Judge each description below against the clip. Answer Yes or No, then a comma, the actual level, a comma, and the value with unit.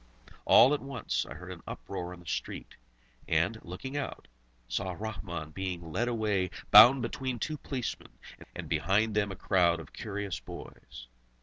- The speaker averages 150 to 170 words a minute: Yes, average, 160 wpm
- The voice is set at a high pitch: No, very low, 95 Hz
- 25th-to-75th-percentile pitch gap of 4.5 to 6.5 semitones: Yes, average, 4.9 semitones